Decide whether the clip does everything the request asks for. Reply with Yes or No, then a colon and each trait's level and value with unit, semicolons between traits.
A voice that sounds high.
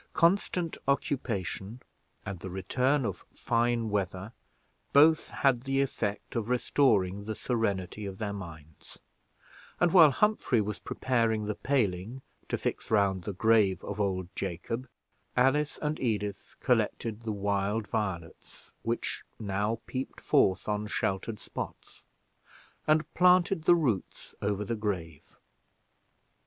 No: low, 110 Hz